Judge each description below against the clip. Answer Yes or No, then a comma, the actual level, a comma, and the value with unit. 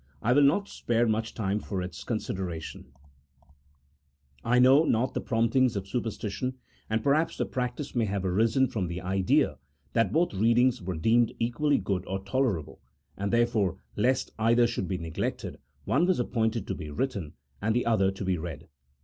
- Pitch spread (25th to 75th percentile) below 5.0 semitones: Yes, average, 4.5 semitones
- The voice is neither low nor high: No, low, 110 Hz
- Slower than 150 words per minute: No, average, 175 wpm